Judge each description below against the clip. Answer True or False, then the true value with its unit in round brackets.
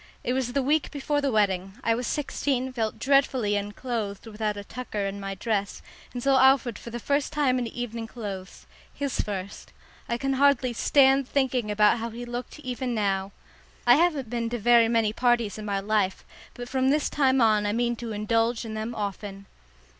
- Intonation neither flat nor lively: True (3.7 semitones)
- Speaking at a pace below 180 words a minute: False (190 wpm)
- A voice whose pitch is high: True (235 Hz)